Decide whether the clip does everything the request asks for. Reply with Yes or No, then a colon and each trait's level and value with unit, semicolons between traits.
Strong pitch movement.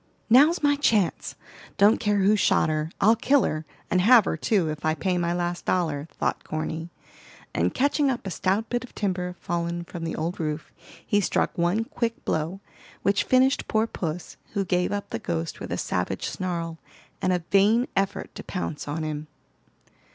No: average, 4.8 semitones